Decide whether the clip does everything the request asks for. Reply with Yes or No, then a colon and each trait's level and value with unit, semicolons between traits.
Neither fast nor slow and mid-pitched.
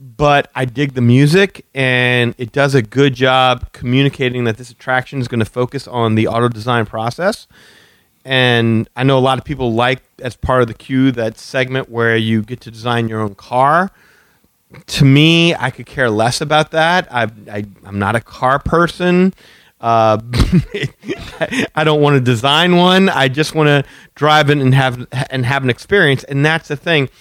No: average, 185 wpm; low, 130 Hz